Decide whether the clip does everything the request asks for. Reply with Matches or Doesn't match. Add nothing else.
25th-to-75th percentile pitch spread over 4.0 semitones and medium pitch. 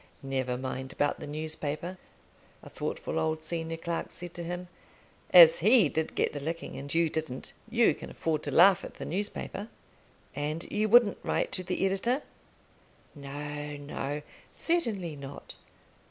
Matches